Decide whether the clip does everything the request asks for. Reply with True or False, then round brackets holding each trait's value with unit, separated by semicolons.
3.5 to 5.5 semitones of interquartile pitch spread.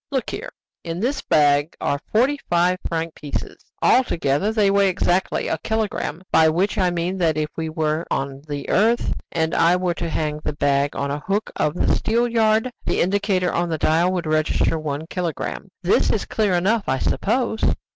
True (4.9 semitones)